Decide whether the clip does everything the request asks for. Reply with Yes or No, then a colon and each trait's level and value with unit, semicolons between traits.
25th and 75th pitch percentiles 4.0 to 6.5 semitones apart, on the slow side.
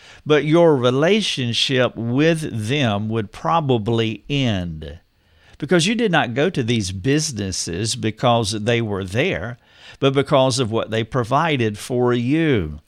Yes: average, 4.5 semitones; slow, 130 wpm